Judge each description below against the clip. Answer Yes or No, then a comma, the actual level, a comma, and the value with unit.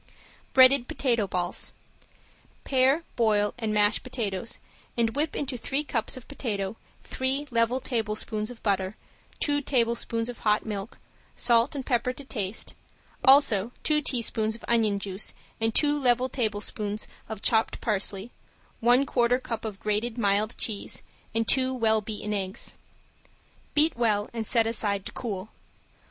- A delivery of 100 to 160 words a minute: Yes, average, 140 wpm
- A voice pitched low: No, high, 230 Hz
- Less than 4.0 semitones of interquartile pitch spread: Yes, average, 3.3 semitones